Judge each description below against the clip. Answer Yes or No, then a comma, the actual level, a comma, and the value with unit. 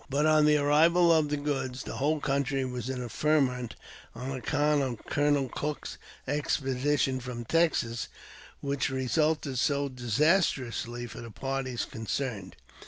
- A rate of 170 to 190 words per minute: No, average, 140 wpm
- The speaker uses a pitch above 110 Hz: Yes, low, 135 Hz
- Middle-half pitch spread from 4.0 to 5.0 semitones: No, average, 2.9 semitones